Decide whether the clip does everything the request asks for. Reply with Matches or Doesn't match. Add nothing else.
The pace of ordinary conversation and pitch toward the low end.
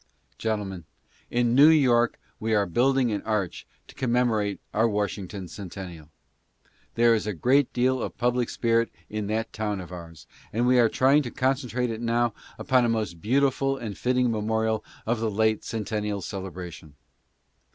Matches